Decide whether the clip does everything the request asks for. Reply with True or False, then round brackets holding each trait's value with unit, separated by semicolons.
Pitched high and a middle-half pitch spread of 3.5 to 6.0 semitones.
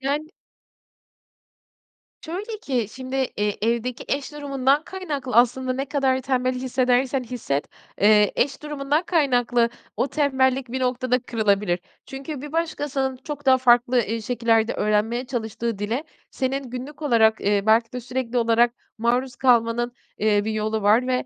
False (250 Hz; 2.8 semitones)